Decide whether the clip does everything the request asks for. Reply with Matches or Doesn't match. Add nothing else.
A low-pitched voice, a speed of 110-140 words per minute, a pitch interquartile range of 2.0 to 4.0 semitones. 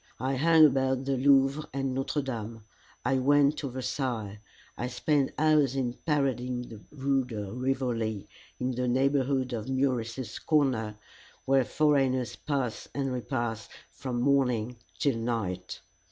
Matches